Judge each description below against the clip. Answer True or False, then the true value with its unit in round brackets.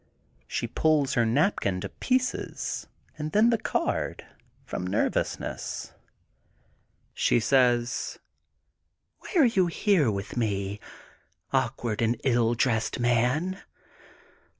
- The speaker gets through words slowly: True (105 wpm)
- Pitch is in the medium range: False (125 Hz)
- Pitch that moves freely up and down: True (6.8 semitones)